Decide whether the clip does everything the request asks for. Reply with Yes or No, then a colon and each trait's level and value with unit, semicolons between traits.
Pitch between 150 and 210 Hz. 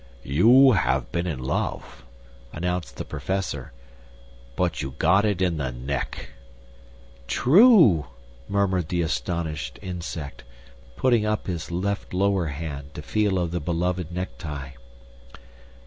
No: very low, 85 Hz